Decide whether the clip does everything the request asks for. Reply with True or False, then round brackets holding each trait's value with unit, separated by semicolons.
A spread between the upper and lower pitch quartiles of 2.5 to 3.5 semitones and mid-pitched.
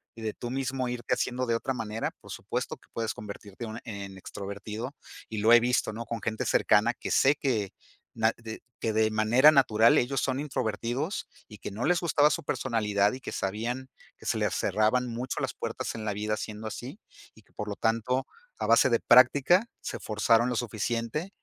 False (2.9 semitones; 115 Hz)